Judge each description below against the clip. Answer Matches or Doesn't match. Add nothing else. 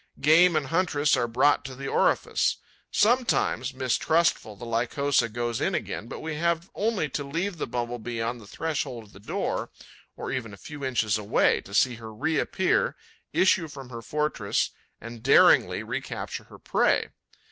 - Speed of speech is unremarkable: Matches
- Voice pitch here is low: Matches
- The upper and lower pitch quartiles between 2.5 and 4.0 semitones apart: Doesn't match